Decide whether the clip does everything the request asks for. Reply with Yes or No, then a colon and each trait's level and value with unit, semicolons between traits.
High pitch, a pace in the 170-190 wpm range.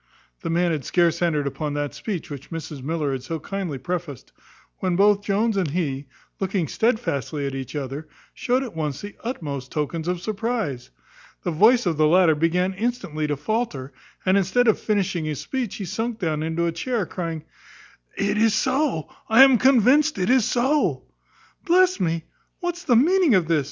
No: medium, 180 Hz; average, 180 wpm